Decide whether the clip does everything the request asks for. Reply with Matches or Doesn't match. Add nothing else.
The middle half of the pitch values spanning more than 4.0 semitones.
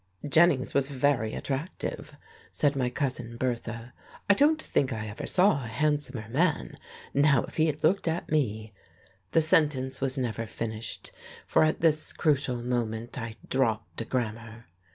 Matches